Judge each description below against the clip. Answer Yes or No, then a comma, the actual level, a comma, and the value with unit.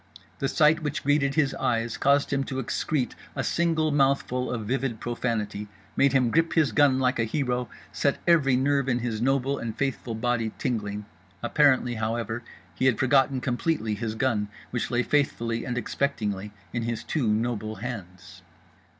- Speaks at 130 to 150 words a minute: No, average, 165 wpm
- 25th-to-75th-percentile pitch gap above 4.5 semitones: No, average, 3.4 semitones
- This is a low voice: Yes, low, 125 Hz